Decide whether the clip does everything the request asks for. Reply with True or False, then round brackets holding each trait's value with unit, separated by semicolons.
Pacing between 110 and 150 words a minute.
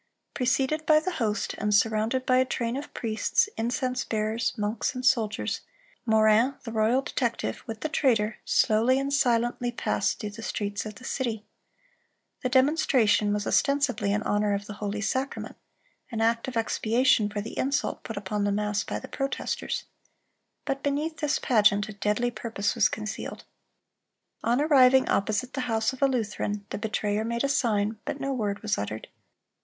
False (170 wpm)